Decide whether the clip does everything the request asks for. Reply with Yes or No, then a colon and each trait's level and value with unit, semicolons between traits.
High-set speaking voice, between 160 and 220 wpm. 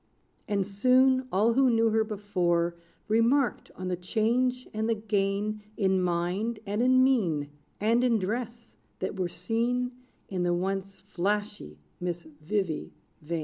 No: high, 210 Hz; average, 145 wpm